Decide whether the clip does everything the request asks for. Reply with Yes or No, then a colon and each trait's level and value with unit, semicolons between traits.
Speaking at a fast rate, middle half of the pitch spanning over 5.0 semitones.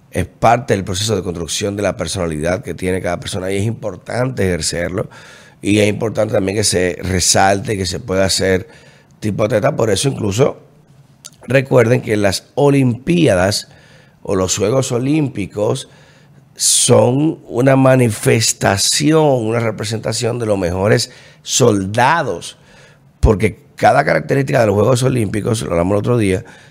No: average, 140 wpm; wide, 5.5 semitones